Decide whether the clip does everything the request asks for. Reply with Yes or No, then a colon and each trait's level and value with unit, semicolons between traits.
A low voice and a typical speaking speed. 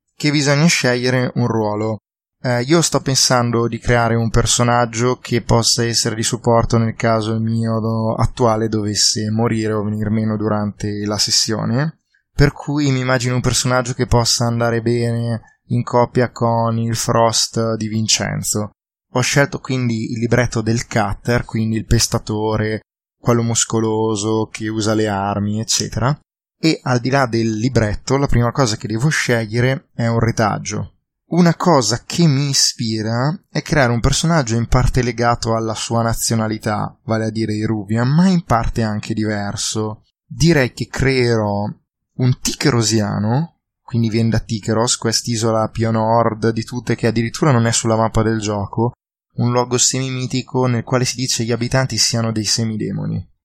Yes: low, 115 Hz; average, 155 wpm